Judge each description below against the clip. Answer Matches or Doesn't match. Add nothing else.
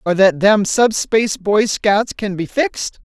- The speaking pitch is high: Matches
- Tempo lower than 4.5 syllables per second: Matches